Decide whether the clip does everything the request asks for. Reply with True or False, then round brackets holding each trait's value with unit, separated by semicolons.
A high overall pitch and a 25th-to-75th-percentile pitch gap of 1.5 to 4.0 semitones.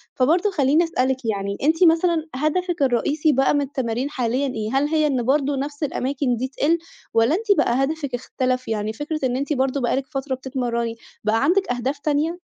True (270 Hz; 3.3 semitones)